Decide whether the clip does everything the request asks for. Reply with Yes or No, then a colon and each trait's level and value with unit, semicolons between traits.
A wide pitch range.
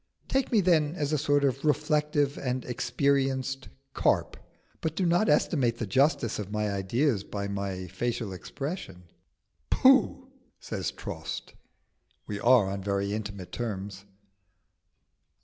Yes: wide, 6.8 semitones